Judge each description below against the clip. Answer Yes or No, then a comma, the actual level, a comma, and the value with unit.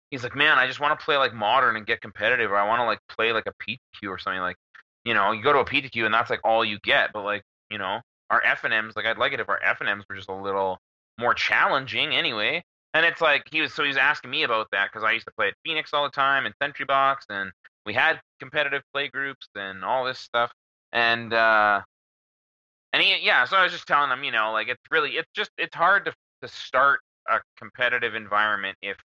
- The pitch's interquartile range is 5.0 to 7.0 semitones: Yes, wide, 5.4 semitones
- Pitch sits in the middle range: No, low, 120 Hz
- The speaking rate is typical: No, fast, 250 wpm